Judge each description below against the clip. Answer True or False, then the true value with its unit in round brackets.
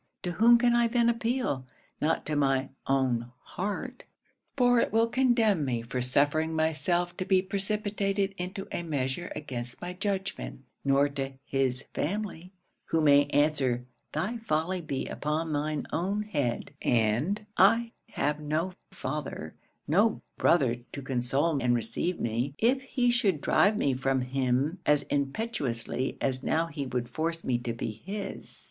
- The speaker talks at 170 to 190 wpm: False (150 wpm)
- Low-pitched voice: False (155 Hz)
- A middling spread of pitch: False (6.8 semitones)